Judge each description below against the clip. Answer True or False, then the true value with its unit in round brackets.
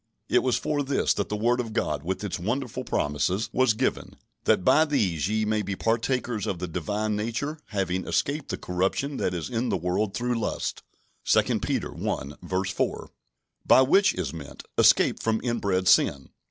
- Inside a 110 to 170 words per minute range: False (180 wpm)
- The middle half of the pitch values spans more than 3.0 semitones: True (5.0 semitones)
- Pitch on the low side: True (105 Hz)